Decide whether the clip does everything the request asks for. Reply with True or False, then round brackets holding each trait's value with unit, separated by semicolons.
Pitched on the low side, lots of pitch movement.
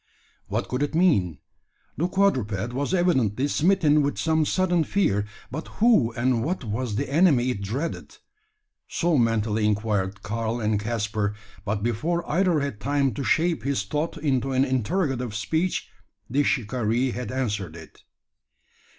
True (130 Hz; 6.5 semitones)